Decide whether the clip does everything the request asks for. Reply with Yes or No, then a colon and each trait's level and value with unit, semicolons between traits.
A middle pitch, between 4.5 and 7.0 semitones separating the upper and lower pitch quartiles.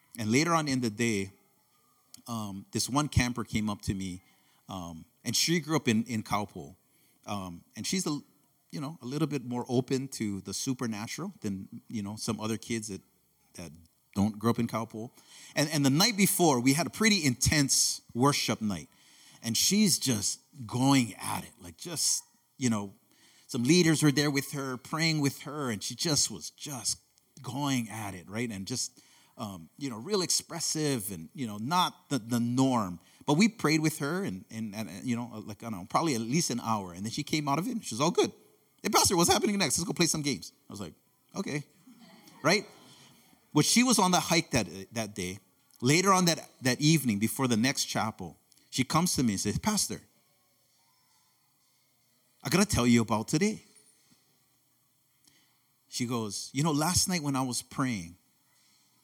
No: low, 130 Hz; average, 5.2 semitones